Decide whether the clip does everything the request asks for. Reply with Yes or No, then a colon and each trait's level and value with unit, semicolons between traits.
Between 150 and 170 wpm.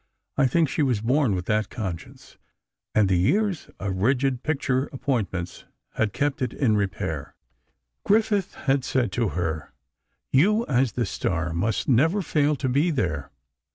Yes: average, 155 wpm